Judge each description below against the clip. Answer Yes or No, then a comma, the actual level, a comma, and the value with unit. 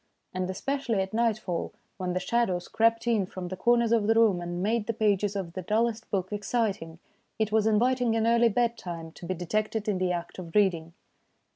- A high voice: Yes, high, 210 Hz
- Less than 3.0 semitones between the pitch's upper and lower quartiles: No, average, 3.8 semitones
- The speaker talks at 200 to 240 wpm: Yes, fast, 205 wpm